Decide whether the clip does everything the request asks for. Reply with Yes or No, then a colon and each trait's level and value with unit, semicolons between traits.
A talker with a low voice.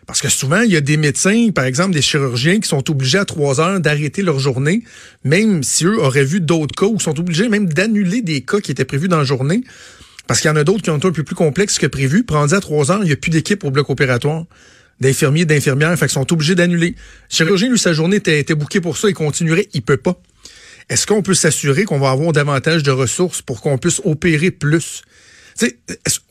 No: medium, 160 Hz